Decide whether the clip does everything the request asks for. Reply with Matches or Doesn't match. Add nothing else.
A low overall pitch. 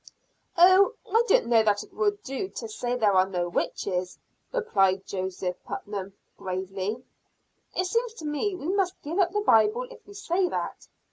Doesn't match